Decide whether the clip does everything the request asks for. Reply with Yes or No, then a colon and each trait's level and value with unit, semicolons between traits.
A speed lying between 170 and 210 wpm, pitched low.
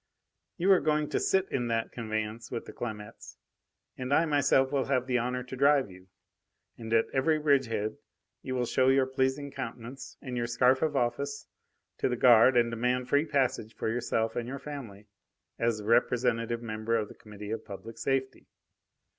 Yes: average, 180 wpm; low, 125 Hz